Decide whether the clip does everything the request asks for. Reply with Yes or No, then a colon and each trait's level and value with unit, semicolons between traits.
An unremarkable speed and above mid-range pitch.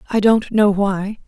Yes: average, 190 wpm; high, 205 Hz